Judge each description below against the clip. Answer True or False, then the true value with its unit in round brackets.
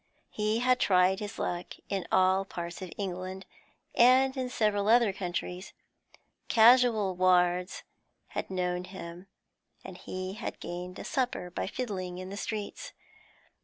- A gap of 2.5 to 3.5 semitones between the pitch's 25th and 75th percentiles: True (3.1 semitones)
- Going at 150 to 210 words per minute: False (135 wpm)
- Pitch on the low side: False (190 Hz)